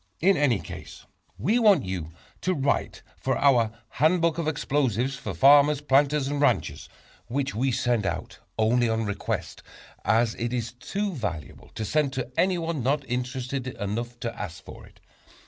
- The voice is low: Yes, low, 130 Hz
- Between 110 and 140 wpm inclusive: No, average, 160 wpm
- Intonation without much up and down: No, average, 4.2 semitones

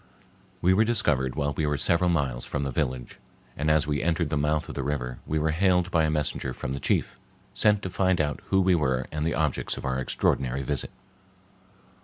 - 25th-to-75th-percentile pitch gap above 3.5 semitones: Yes, average, 3.9 semitones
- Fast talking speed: Yes, fast, 215 wpm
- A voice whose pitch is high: No, very low, 75 Hz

